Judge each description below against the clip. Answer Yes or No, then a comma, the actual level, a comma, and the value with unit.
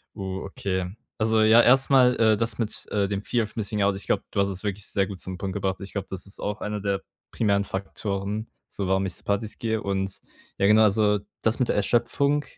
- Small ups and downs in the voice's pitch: Yes, narrow, 2.2 semitones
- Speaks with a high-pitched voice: No, low, 100 Hz